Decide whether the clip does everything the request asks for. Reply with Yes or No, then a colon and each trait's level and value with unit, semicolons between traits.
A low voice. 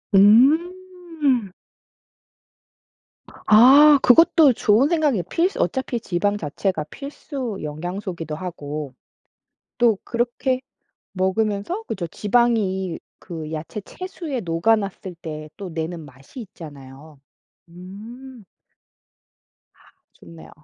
No: high, 205 Hz